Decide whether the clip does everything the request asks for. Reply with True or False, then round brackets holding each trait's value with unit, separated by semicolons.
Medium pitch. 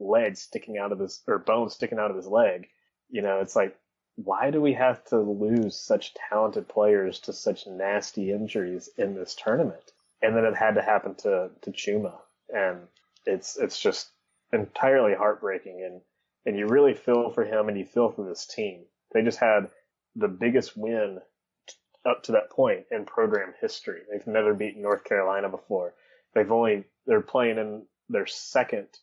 False (110 Hz)